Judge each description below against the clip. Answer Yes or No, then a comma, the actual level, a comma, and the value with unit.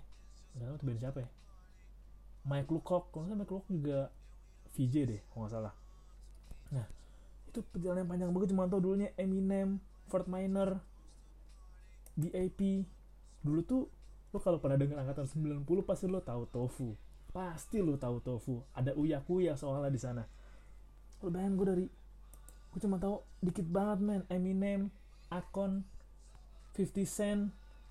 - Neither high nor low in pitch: Yes, medium, 175 Hz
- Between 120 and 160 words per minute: Yes, fast, 140 wpm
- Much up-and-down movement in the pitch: Yes, wide, 6.4 semitones